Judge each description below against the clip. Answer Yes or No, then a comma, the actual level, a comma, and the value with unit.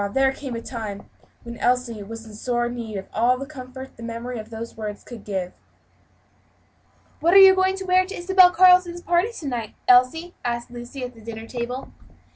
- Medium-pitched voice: No, very high, 250 Hz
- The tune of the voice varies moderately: No, wide, 6.8 semitones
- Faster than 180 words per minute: Yes, average, 190 wpm